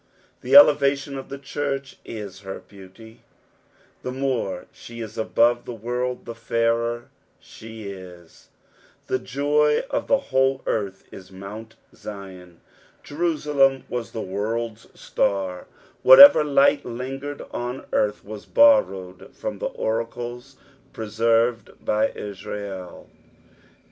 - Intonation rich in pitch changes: No, average, 4.6 semitones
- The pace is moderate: No, slow, 120 wpm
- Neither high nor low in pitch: No, low, 115 Hz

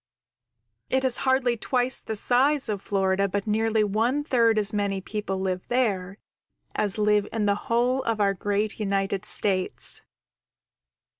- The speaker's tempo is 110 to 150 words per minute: Yes, average, 145 wpm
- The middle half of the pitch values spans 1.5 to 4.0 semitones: Yes, average, 3.3 semitones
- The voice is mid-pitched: No, high, 210 Hz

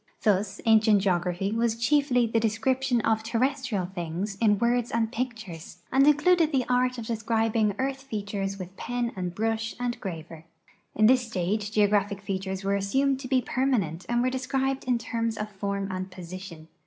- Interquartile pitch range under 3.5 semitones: No, average, 4.2 semitones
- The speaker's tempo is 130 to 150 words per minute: No, average, 165 wpm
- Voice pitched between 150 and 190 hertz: No, high, 220 Hz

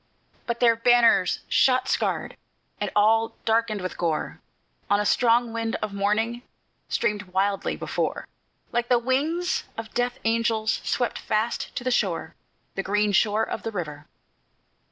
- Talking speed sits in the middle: Yes, average, 145 wpm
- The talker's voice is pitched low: No, high, 225 Hz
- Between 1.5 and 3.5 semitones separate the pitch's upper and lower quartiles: Yes, narrow, 2.6 semitones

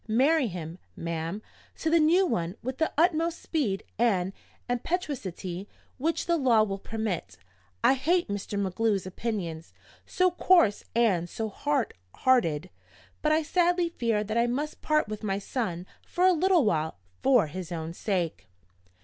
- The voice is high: Yes, high, 225 Hz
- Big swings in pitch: Yes, wide, 8.6 semitones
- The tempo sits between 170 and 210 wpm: No, average, 150 wpm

